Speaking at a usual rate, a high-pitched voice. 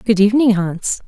Yes: average, 170 wpm; high, 210 Hz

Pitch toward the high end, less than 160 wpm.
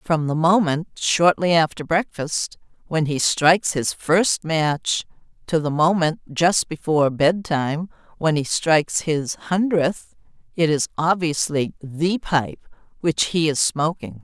No: medium, 160 Hz; average, 140 wpm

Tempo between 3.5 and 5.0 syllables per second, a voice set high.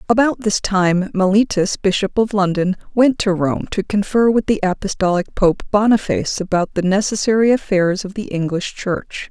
Yes: 4.9 syllables/s; high, 200 Hz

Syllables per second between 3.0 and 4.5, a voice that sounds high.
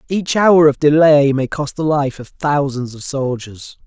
No: 4.1 syllables/s; medium, 145 Hz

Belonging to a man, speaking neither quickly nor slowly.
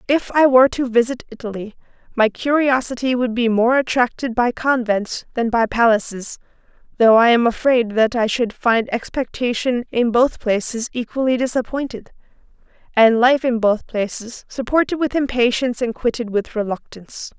No: female; average, 150 wpm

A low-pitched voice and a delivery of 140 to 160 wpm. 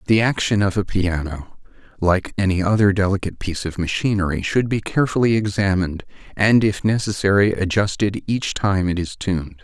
Yes: very low, 95 Hz; average, 155 wpm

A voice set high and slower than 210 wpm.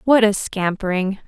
Yes: high, 200 Hz; average, 140 wpm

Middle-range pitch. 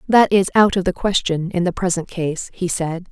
Yes: medium, 180 Hz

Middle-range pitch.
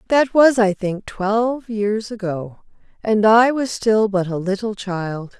No: high, 210 Hz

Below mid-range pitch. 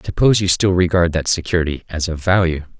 Yes: very low, 85 Hz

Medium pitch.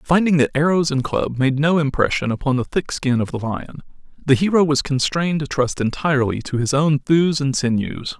Yes: medium, 145 Hz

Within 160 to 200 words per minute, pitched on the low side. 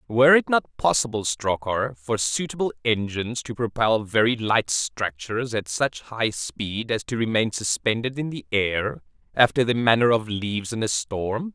Yes: average, 165 wpm; low, 115 Hz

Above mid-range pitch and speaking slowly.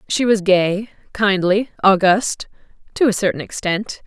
Yes: high, 200 Hz; slow, 120 wpm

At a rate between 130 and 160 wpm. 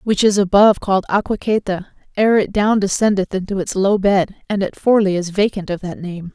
No: average, 200 wpm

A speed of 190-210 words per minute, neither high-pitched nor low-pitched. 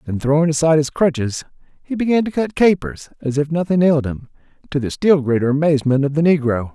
Yes: fast, 205 wpm; medium, 150 Hz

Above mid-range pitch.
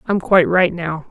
No: medium, 175 Hz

